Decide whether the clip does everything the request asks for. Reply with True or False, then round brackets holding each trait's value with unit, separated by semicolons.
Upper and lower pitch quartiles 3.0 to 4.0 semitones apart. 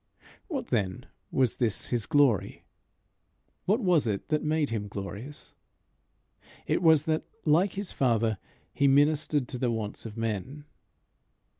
False (5.5 semitones)